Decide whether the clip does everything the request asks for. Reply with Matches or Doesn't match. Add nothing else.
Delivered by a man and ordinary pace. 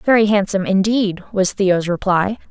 Doesn't match